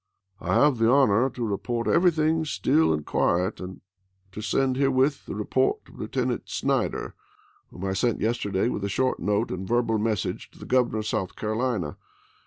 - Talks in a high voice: No, low, 115 Hz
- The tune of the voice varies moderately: Yes, average, 4.5 semitones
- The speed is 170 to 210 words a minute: Yes, average, 180 wpm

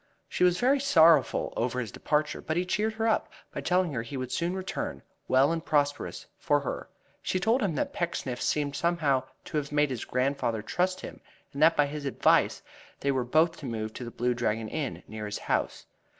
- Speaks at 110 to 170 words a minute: No, fast, 205 wpm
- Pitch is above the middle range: No, medium, 145 Hz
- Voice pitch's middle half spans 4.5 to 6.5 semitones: Yes, wide, 5.5 semitones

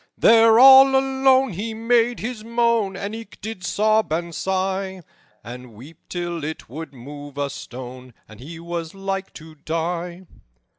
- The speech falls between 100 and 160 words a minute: Yes, average, 150 wpm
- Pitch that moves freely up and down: Yes, wide, 6.1 semitones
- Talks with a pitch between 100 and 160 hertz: No, medium, 185 Hz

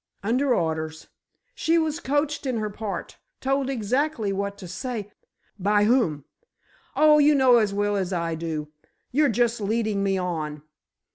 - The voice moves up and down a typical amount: No, wide, 6.0 semitones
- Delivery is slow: No, average, 150 wpm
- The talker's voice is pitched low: No, high, 210 Hz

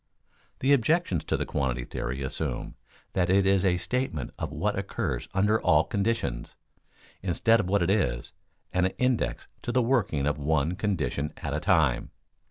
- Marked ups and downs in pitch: Yes, wide, 7.2 semitones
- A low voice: Yes, very low, 90 Hz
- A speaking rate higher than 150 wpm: Yes, average, 170 wpm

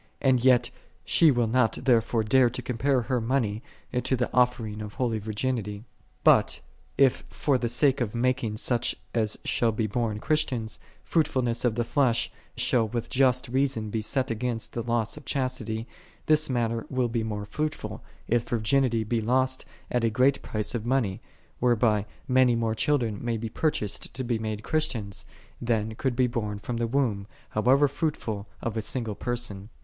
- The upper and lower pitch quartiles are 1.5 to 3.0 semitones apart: Yes, average, 2.7 semitones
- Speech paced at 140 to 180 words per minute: Yes, average, 175 wpm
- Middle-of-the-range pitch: No, low, 120 Hz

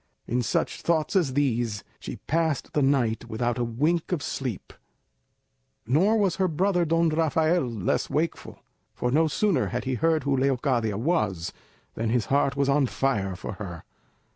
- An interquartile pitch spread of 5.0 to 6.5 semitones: Yes, wide, 5.5 semitones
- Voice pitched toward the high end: No, medium, 140 Hz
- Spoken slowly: No, average, 165 wpm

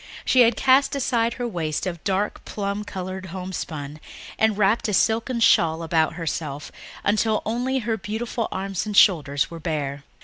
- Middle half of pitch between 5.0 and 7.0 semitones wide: Yes, wide, 5.4 semitones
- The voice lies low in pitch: No, high, 195 Hz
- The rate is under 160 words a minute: No, average, 165 wpm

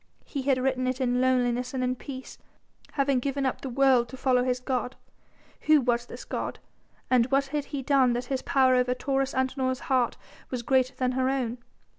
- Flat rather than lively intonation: Yes, narrow, 1.3 semitones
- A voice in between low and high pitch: No, very high, 255 Hz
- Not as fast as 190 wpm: No, average, 195 wpm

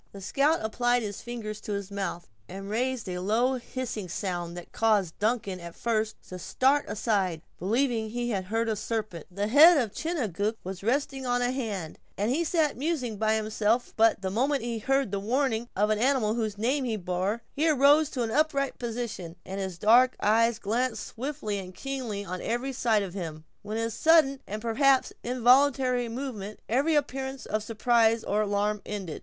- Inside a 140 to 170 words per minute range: No, average, 185 wpm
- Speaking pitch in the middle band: No, high, 225 Hz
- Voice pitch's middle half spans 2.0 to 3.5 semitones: No, average, 4.1 semitones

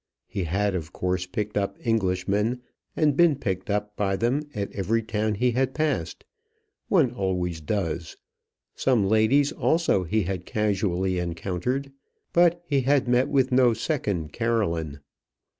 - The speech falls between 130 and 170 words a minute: Yes, average, 140 wpm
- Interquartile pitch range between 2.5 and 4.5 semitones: No, wide, 5.5 semitones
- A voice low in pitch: Yes, low, 105 Hz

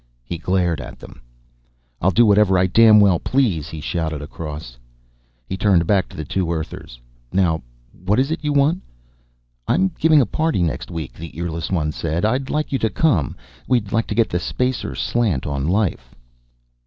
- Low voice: Yes, very low, 95 Hz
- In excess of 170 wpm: Yes, average, 180 wpm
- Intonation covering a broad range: Yes, wide, 6.4 semitones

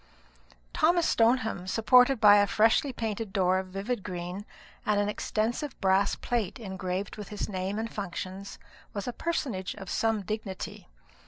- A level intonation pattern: No, average, 3.1 semitones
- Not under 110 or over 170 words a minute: Yes, average, 155 wpm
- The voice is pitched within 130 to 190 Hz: No, high, 205 Hz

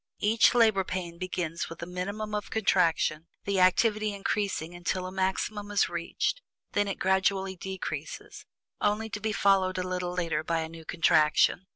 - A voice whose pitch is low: No, high, 190 Hz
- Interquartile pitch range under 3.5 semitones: Yes, average, 2.9 semitones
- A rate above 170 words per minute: No, average, 165 wpm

